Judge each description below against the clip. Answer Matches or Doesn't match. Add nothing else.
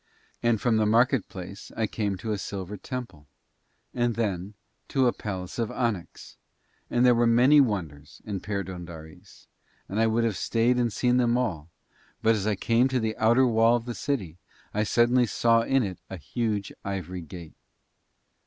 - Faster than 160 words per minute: Matches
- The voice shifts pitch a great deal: Doesn't match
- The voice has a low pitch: Matches